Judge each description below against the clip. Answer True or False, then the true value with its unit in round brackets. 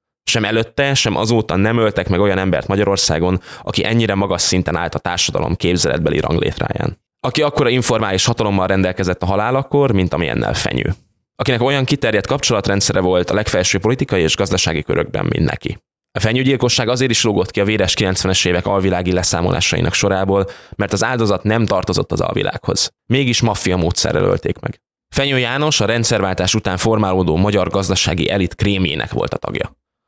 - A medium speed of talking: False (160 wpm)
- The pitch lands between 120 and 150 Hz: False (100 Hz)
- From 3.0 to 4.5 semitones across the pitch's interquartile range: True (4.0 semitones)